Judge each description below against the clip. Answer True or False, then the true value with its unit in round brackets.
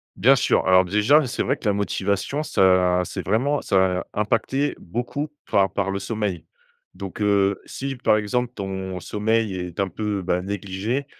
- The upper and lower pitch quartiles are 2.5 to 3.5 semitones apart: False (4.0 semitones)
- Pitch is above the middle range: False (100 Hz)